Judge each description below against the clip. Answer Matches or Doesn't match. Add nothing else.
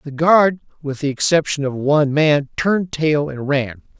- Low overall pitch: Doesn't match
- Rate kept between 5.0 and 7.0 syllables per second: Doesn't match